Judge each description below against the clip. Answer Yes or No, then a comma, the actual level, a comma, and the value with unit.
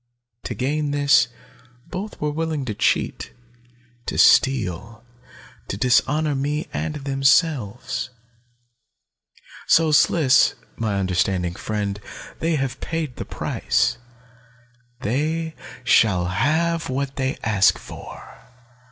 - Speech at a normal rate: No, slow, 100 wpm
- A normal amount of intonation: No, wide, 5.9 semitones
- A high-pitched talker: No, low, 135 Hz